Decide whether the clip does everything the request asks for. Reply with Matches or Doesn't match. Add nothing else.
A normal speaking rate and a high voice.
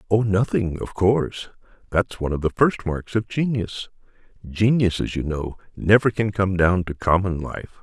Doesn't match